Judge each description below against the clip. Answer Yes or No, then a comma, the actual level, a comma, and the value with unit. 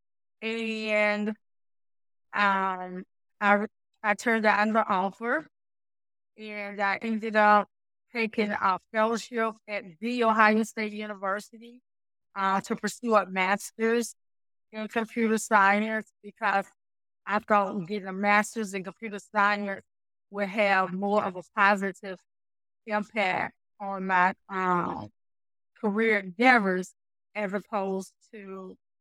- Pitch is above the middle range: Yes, high, 205 Hz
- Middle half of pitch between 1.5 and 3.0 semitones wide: Yes, narrow, 2.4 semitones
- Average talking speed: No, slow, 110 wpm